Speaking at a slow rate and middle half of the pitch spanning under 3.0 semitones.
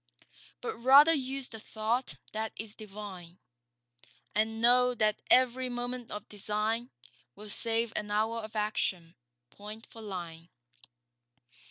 Yes: slow, 125 wpm; narrow, 2.6 semitones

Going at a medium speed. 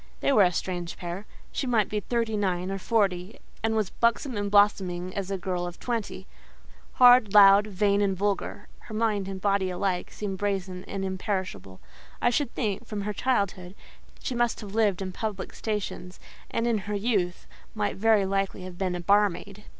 Yes: average, 180 wpm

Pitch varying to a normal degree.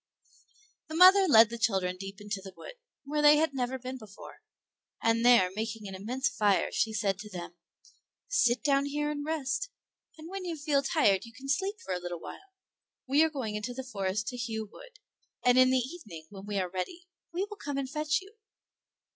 No: wide, 6.4 semitones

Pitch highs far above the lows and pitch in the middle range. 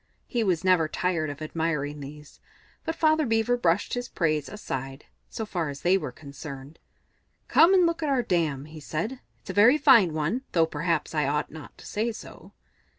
Yes: wide, 7.1 semitones; medium, 165 Hz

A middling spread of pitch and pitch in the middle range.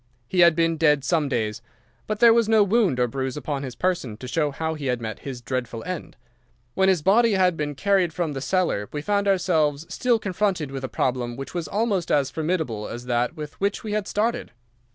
No: wide, 6.3 semitones; medium, 160 Hz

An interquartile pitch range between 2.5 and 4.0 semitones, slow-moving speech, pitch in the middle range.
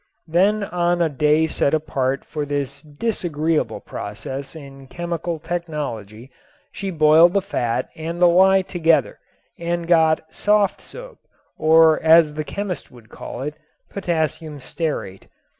Yes: average, 3.1 semitones; slow, 130 wpm; medium, 160 Hz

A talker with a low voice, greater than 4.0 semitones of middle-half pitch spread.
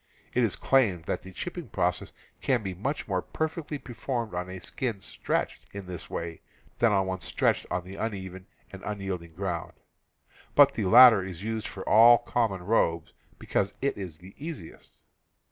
Yes: low, 100 Hz; average, 4.5 semitones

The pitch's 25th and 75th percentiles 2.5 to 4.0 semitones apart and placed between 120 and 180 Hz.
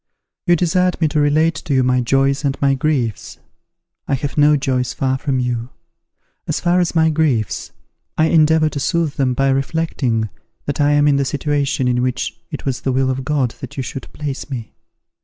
Yes: average, 2.9 semitones; medium, 140 Hz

